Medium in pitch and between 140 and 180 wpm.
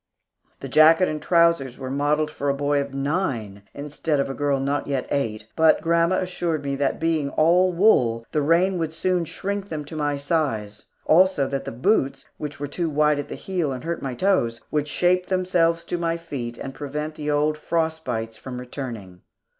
No: medium, 150 Hz; average, 195 wpm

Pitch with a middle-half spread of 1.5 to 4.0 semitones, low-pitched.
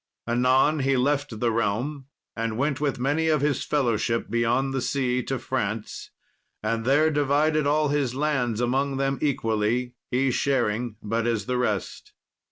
Yes: average, 3.5 semitones; low, 130 Hz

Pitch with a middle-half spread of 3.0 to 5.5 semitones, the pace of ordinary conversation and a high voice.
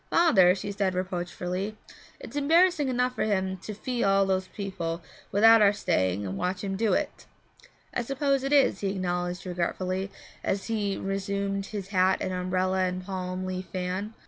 No: narrow, 2.6 semitones; average, 170 wpm; high, 195 Hz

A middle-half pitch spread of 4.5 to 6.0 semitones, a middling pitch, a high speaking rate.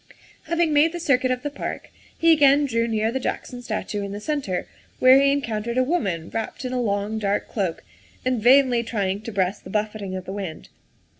No: average, 5.0 semitones; high, 230 Hz; fast, 210 wpm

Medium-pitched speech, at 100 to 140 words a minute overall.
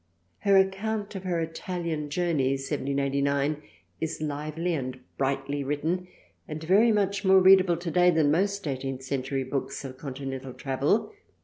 Yes: medium, 155 Hz; slow, 135 wpm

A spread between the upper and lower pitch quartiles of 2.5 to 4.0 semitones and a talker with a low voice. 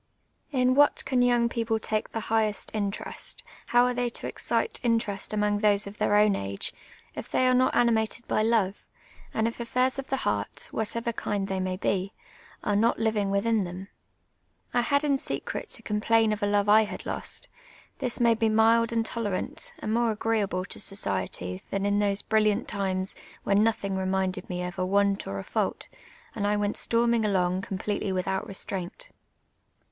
No: average, 2.9 semitones; high, 210 Hz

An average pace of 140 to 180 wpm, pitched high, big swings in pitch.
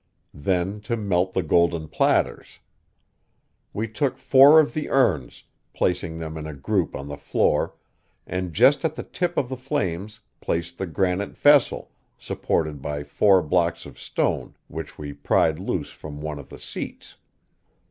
No: average, 160 wpm; very low, 90 Hz; wide, 5.9 semitones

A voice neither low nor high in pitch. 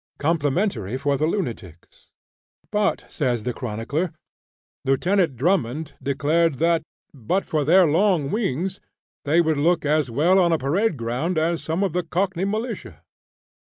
Yes: medium, 160 Hz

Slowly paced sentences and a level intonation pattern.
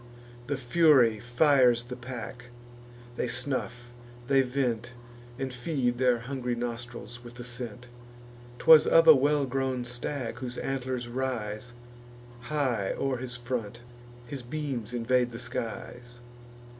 Yes: slow, 125 wpm; narrow, 1.7 semitones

